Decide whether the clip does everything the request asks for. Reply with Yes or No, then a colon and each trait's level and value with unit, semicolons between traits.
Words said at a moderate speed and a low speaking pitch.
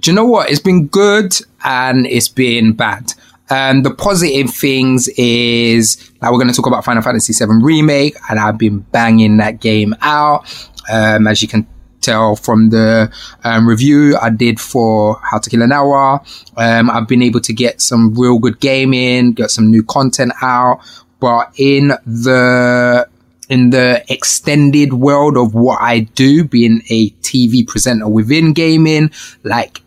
Yes: average, 170 wpm; low, 125 Hz